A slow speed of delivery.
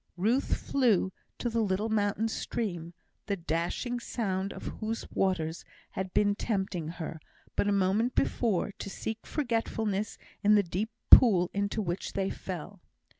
No: average, 145 wpm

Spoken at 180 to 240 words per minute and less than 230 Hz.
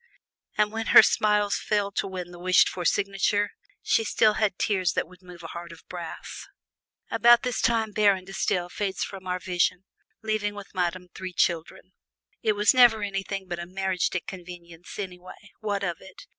Yes: average, 185 wpm; high, 190 Hz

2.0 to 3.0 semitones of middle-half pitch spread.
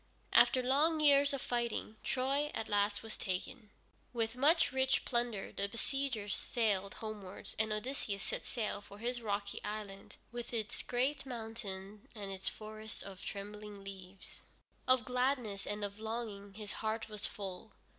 No: average, 3.6 semitones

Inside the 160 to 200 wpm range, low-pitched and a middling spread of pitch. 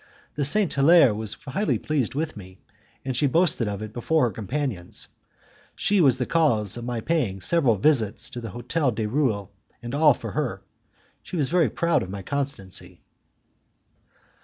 No: average, 170 wpm; low, 130 Hz; wide, 6.1 semitones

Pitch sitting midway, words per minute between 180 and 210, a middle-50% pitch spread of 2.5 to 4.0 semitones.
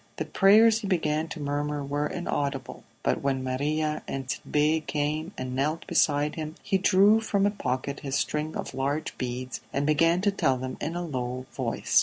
Yes: medium, 150 Hz; average, 185 wpm; average, 3.4 semitones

